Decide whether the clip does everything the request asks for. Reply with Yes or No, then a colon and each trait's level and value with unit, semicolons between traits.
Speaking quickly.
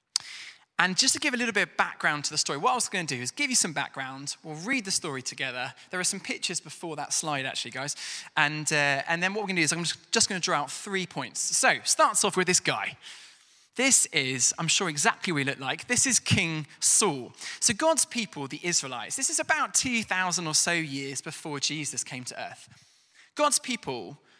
Yes: fast, 225 wpm